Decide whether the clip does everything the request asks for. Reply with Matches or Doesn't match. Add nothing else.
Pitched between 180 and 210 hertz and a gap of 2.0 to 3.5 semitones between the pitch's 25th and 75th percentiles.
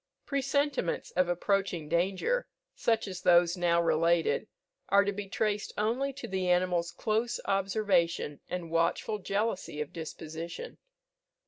Doesn't match